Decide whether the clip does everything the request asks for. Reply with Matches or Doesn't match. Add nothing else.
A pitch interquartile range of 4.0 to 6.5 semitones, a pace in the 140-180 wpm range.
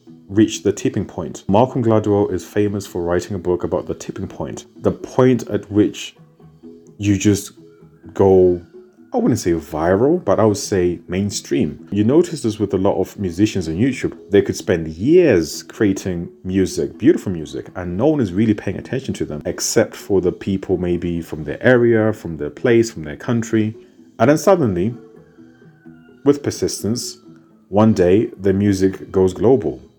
Matches